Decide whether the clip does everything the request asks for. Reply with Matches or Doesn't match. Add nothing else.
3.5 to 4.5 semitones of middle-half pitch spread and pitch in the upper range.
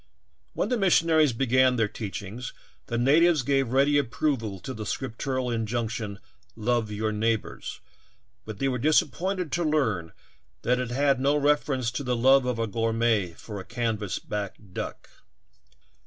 Doesn't match